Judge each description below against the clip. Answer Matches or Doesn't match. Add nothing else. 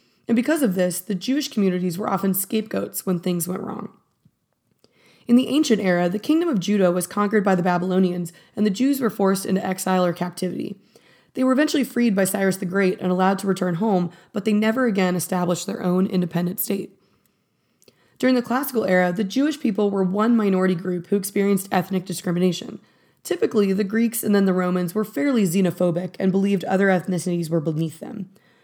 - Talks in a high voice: Matches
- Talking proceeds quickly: Doesn't match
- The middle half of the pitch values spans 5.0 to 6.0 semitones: Doesn't match